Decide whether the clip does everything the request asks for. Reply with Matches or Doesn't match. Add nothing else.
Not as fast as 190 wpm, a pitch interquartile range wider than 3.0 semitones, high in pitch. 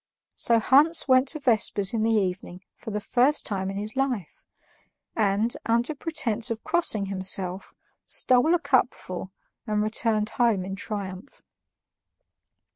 Matches